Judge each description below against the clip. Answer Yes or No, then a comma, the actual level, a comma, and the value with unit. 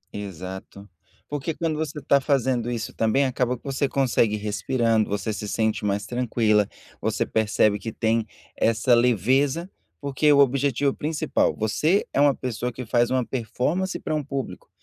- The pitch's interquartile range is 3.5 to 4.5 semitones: Yes, average, 4.2 semitones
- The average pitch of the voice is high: No, low, 125 Hz